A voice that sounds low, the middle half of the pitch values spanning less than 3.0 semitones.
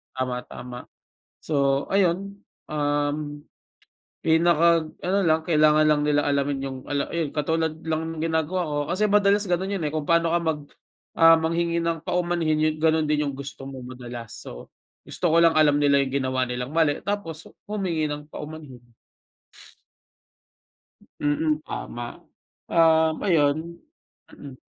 No: medium, 155 Hz; narrow, 2.6 semitones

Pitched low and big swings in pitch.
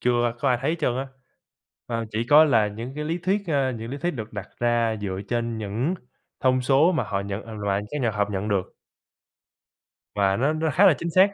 Yes: low, 120 Hz; wide, 5.7 semitones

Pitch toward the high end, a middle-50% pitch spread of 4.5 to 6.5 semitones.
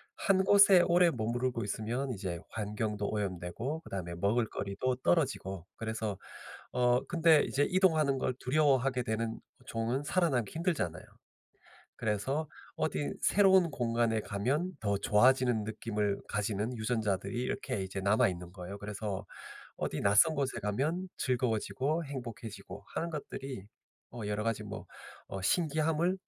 No: low, 120 Hz; wide, 6.0 semitones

